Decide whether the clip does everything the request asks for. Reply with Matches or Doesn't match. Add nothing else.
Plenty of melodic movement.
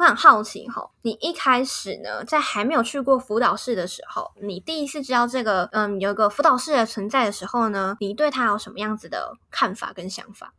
Doesn't match